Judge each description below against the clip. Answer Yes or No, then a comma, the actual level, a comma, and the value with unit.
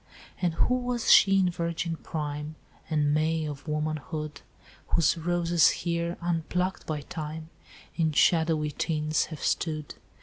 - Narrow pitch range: Yes, narrow, 2.0 semitones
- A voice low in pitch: No, medium, 160 Hz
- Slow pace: Yes, slow, 130 wpm